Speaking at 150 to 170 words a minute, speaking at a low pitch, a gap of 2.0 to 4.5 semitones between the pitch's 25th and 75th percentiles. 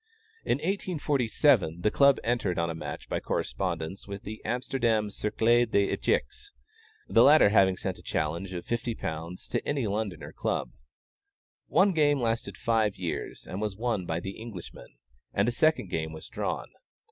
No: average, 160 wpm; low, 105 Hz; average, 5.0 semitones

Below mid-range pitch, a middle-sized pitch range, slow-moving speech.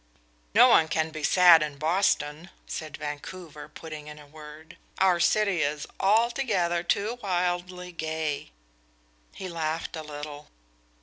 No: medium, 160 Hz; average, 3.1 semitones; slow, 130 wpm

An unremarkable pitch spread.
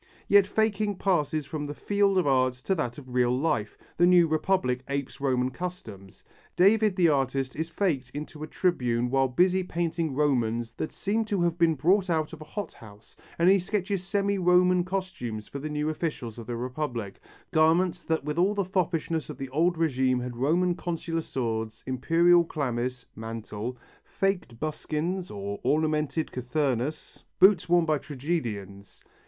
No: wide, 5.9 semitones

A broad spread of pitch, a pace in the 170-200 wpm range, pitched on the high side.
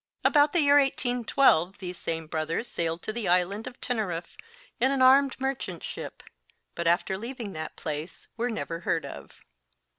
No: wide, 7.3 semitones; average, 160 wpm; high, 210 Hz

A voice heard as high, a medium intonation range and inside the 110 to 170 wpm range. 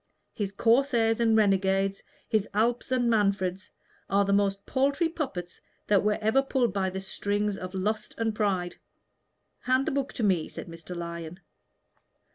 Yes: high, 205 Hz; average, 3.4 semitones; average, 155 wpm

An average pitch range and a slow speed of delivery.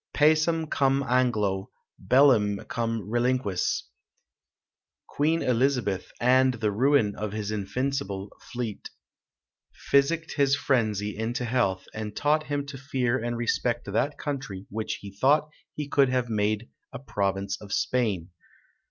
Yes: average, 4.9 semitones; slow, 125 wpm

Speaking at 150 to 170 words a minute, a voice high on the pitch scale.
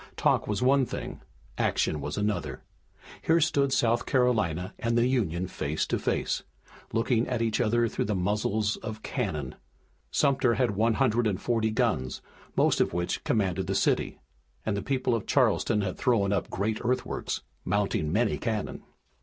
No: average, 160 wpm; low, 110 Hz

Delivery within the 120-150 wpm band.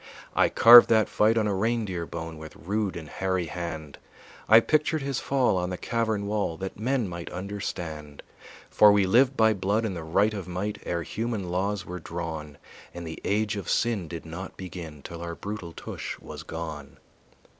No: average, 185 wpm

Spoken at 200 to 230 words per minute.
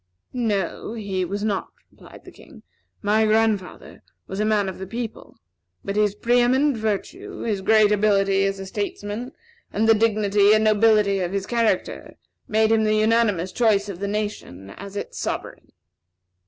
No: average, 165 wpm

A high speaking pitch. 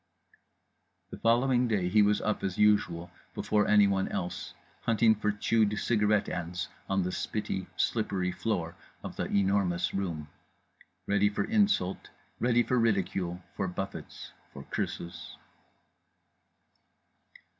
No: low, 100 Hz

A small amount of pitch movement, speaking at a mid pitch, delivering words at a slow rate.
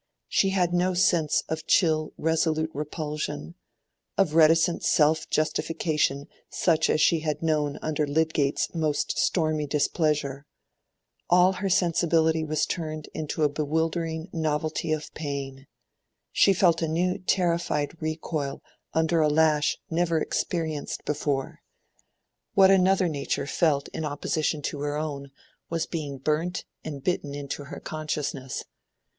Yes: narrow, 2.0 semitones; medium, 155 Hz; slow, 125 wpm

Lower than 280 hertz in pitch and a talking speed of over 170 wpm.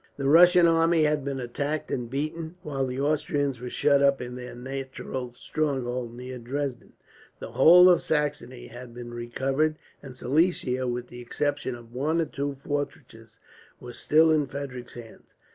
No: low, 135 Hz; average, 160 wpm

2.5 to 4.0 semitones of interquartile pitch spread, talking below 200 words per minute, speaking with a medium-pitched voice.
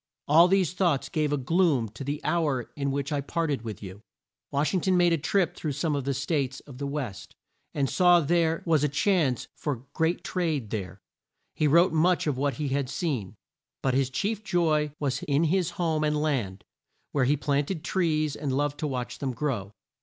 No: average, 3.6 semitones; fast, 205 wpm; medium, 145 Hz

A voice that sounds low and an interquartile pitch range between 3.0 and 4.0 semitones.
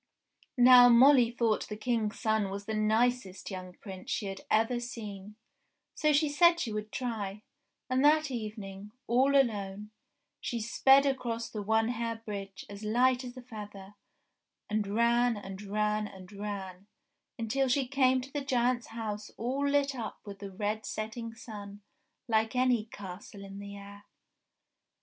No: high, 220 Hz; average, 3.3 semitones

